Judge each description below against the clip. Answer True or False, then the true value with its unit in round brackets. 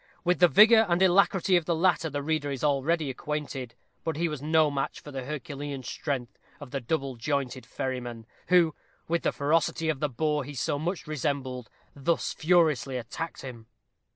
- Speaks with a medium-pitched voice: True (150 Hz)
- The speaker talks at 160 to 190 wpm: True (180 wpm)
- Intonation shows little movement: False (3.5 semitones)